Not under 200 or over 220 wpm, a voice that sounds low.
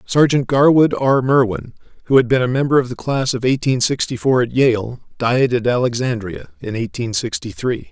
No: average, 190 wpm; low, 125 Hz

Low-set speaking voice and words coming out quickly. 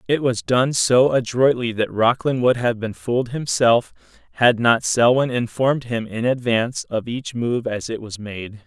No: low, 120 Hz; average, 180 wpm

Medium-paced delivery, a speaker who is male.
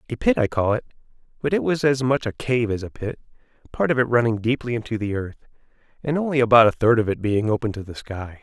No: fast, 250 wpm; male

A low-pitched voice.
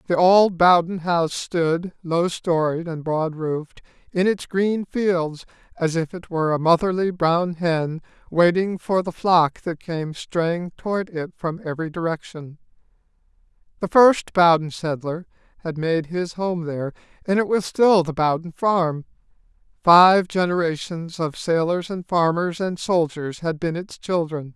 No: medium, 170 Hz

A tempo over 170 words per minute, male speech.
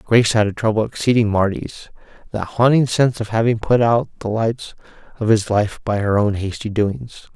Yes: average, 180 wpm; male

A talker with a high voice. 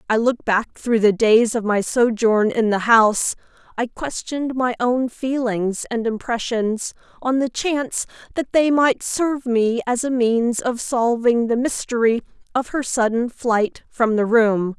Yes: high, 235 Hz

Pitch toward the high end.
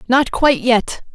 Yes: high, 245 Hz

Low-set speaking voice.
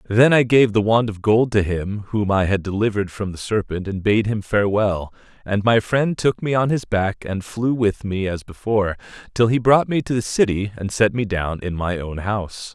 Yes: low, 105 Hz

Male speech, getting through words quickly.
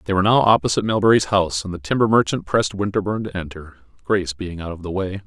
Yes: male; fast, 230 wpm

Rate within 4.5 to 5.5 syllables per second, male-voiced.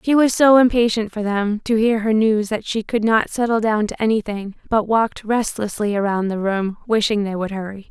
No: 5.2 syllables/s; female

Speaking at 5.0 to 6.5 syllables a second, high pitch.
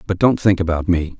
No: 5.7 syllables/s; very low, 90 Hz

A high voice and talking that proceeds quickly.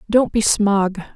No: high, 205 Hz; average, 155 wpm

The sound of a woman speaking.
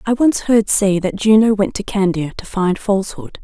Yes: female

